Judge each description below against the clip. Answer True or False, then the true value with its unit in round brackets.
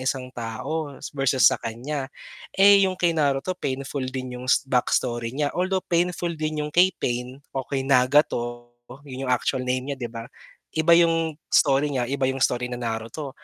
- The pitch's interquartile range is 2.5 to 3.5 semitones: False (3.9 semitones)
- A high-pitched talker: False (135 Hz)